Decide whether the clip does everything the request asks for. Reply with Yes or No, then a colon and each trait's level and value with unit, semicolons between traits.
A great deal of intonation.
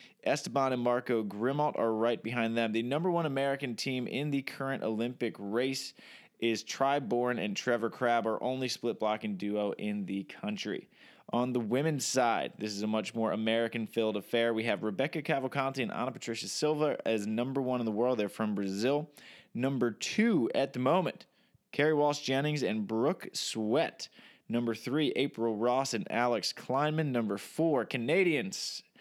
No: average, 3.4 semitones